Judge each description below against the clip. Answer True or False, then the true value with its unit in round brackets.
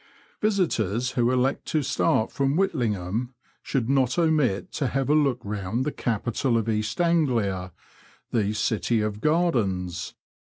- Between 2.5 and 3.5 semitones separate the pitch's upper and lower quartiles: False (4.9 semitones)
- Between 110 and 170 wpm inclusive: True (135 wpm)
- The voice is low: True (120 Hz)